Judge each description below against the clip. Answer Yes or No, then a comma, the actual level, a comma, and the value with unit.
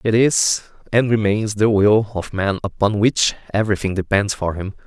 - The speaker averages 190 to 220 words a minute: No, average, 175 wpm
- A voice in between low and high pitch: No, low, 105 Hz